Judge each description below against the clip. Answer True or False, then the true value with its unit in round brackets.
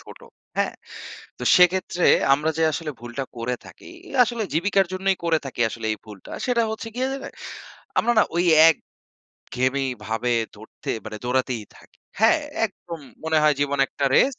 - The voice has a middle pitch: True (155 Hz)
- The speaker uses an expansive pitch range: True (7.1 semitones)